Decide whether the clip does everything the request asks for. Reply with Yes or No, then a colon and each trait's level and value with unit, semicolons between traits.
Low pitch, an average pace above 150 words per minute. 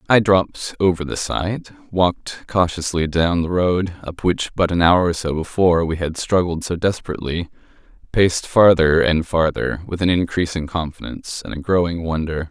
Yes: very low, 85 Hz; average, 170 wpm